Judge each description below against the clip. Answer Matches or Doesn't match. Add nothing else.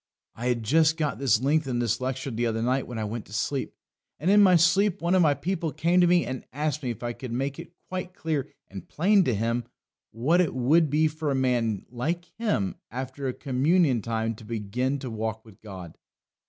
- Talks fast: Matches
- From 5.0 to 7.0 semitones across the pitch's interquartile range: Matches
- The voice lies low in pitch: Matches